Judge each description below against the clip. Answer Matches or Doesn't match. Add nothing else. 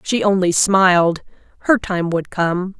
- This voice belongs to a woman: Matches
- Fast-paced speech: Doesn't match